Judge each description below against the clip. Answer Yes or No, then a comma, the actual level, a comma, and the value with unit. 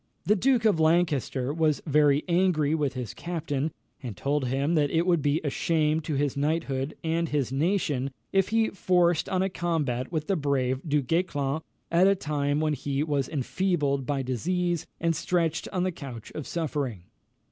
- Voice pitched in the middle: Yes, medium, 155 Hz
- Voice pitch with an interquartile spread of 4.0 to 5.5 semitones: No, average, 3.6 semitones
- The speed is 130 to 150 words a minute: No, average, 180 wpm